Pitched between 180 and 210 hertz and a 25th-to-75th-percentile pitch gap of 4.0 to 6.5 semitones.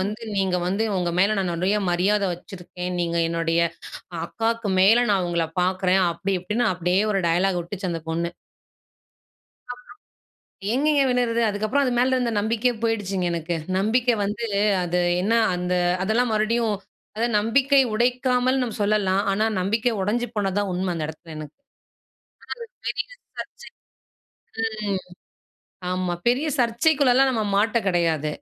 Yes: high, 205 Hz; average, 4.6 semitones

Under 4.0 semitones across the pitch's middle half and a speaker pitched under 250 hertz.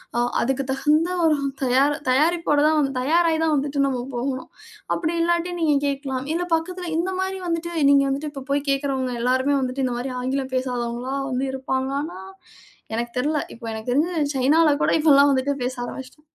No: average, 3.4 semitones; very high, 280 Hz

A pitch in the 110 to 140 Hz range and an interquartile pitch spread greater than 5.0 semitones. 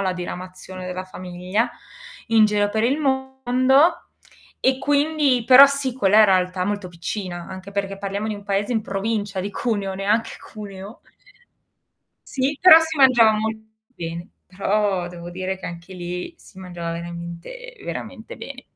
No: high, 205 Hz; wide, 5.4 semitones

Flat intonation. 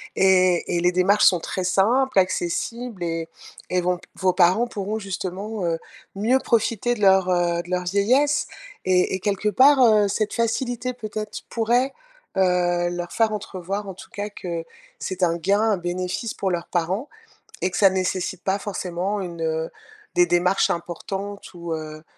No: average, 3.2 semitones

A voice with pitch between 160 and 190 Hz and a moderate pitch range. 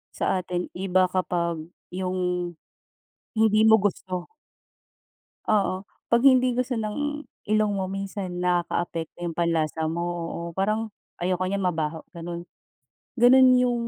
Yes: medium, 185 Hz; average, 3.7 semitones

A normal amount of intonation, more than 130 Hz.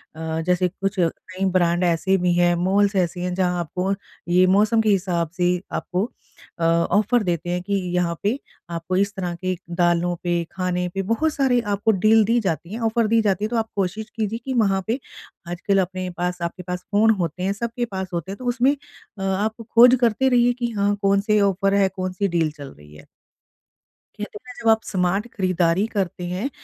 Yes: average, 3.4 semitones; high, 190 Hz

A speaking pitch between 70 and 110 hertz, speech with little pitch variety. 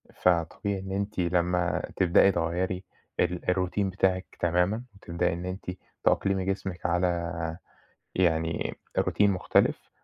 Yes: very low, 90 Hz; narrow, 1.8 semitones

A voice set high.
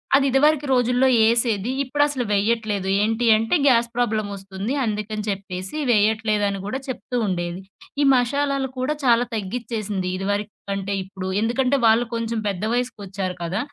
Yes: high, 220 Hz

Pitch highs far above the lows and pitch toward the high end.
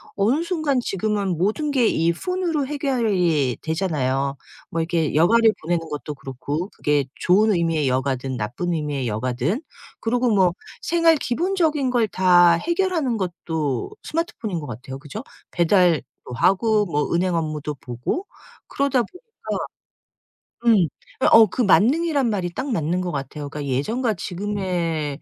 No: wide, 8.1 semitones; medium, 180 Hz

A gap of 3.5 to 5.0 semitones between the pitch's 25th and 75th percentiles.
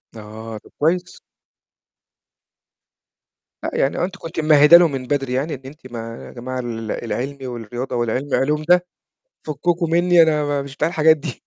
Yes: average, 4.6 semitones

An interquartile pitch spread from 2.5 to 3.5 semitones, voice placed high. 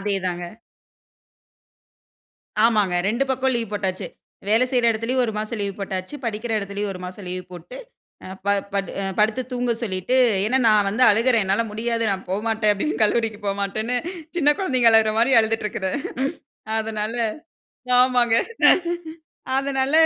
Yes: average, 3.1 semitones; high, 220 Hz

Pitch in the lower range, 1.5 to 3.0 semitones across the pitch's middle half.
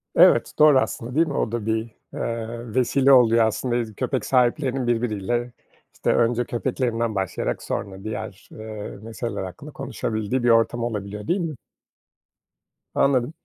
Yes: low, 120 Hz; average, 2.7 semitones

